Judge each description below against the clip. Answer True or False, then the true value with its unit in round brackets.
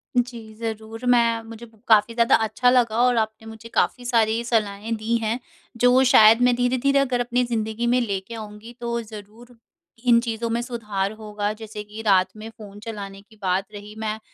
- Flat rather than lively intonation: True (2.0 semitones)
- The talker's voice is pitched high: True (225 Hz)